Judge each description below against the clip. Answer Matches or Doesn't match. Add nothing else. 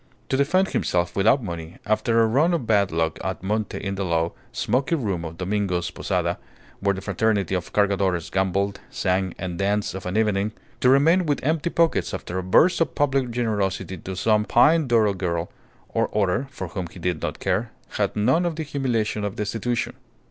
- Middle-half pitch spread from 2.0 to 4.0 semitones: Doesn't match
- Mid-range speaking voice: Doesn't match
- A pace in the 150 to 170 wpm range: Doesn't match